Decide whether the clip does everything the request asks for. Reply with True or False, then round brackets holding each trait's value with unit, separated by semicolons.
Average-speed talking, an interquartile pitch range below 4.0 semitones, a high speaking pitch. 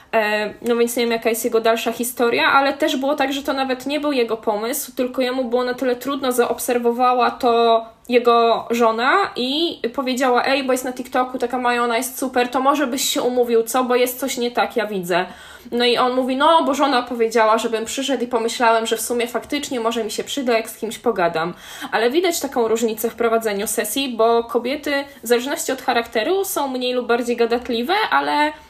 False (205 wpm; 2.7 semitones; 245 Hz)